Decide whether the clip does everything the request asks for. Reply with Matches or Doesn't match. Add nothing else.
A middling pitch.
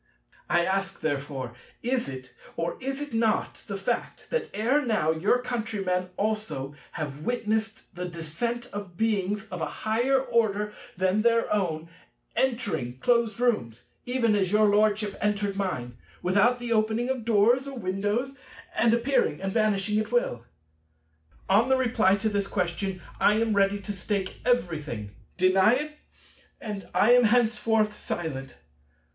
Doesn't match